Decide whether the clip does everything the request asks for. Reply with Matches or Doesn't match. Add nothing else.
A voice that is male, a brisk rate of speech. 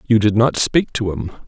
Matches